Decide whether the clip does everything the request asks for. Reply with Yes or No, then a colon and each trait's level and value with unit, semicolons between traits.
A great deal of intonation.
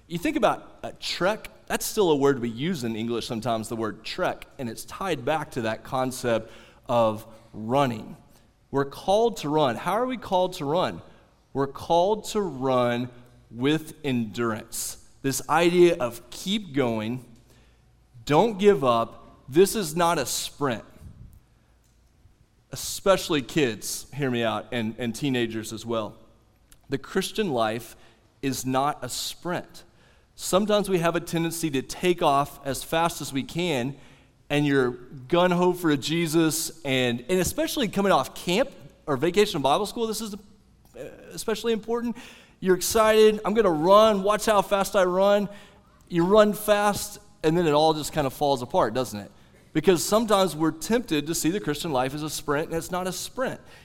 Yes: wide, 7.3 semitones